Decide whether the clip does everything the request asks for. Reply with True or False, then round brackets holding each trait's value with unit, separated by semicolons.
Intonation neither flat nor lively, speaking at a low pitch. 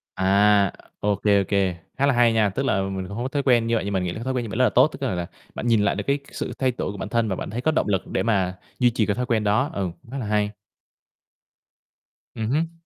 True (3.9 semitones; 110 Hz)